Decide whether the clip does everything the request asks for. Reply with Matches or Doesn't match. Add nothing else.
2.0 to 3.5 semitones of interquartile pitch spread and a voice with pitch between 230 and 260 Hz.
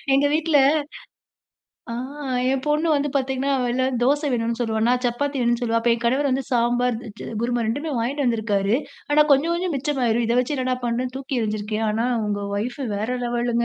Matches